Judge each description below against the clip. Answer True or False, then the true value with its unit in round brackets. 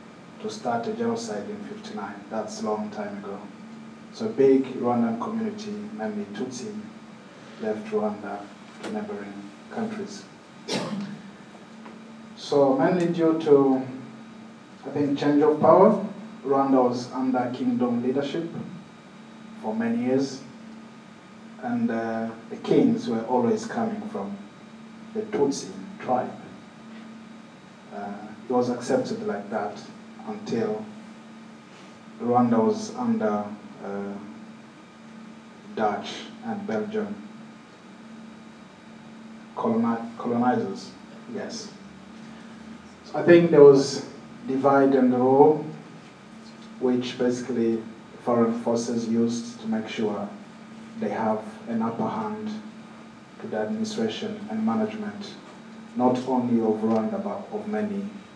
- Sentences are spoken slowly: True (105 wpm)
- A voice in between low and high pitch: False (210 Hz)